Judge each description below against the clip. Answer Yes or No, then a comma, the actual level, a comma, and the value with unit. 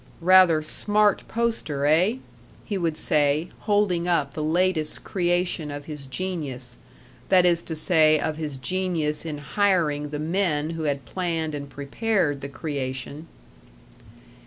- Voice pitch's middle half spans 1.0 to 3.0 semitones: No, average, 3.8 semitones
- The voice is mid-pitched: Yes, medium, 160 Hz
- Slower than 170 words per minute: Yes, slow, 135 wpm